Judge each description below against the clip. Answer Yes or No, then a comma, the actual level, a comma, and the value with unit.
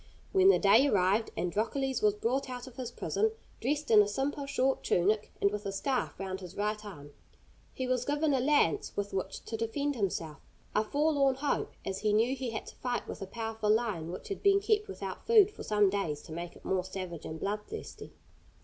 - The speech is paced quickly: Yes, fast, 210 wpm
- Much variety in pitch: Yes, wide, 5.7 semitones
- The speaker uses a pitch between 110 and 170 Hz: No, high, 225 Hz